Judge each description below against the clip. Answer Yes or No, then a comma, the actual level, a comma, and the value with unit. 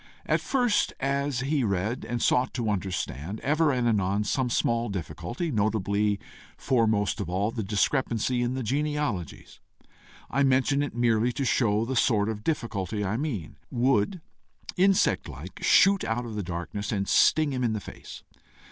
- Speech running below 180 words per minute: Yes, average, 160 wpm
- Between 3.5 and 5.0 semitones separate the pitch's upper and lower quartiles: Yes, average, 4.6 semitones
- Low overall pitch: Yes, low, 115 Hz